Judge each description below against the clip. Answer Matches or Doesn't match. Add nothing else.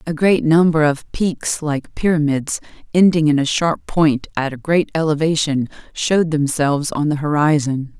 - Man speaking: Doesn't match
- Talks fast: Doesn't match